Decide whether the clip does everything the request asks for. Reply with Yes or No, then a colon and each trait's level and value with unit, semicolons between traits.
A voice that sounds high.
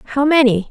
Yes: very high, 260 Hz